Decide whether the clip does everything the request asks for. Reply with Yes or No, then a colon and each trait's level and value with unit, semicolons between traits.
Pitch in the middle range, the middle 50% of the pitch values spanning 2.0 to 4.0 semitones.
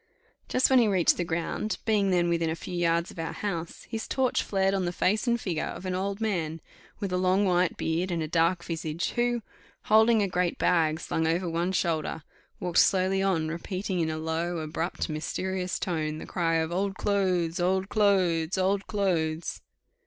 Yes: medium, 180 Hz; average, 2.8 semitones